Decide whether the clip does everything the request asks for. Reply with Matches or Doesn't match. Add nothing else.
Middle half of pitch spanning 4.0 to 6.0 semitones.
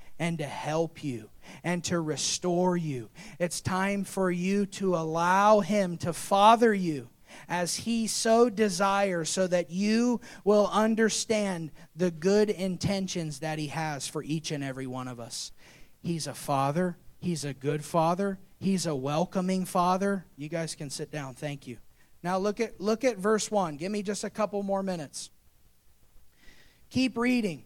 Matches